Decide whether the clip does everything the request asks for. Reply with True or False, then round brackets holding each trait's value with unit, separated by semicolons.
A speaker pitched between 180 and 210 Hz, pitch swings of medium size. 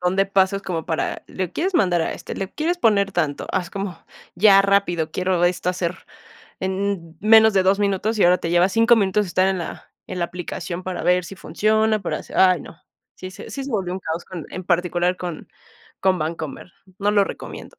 False (185 Hz; 2.2 semitones)